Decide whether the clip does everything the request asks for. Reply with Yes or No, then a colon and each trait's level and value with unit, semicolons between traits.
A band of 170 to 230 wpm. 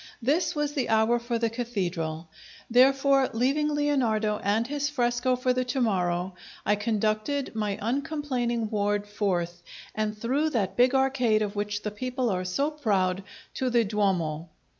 No: average, 155 wpm